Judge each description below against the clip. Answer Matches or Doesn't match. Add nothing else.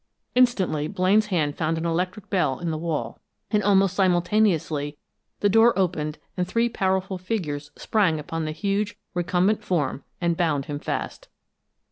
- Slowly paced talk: Doesn't match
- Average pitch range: Matches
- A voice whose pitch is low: Doesn't match